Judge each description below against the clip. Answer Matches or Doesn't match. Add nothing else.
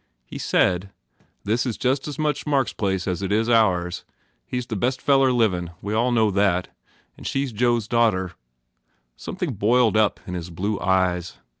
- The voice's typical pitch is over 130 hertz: Doesn't match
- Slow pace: Doesn't match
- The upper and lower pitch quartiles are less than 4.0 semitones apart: Doesn't match